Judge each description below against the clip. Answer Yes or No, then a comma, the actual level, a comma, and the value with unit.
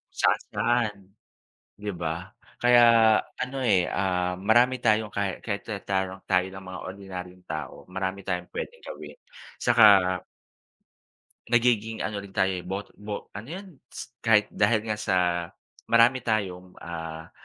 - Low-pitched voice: Yes, low, 100 Hz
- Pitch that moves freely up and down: No, average, 3.8 semitones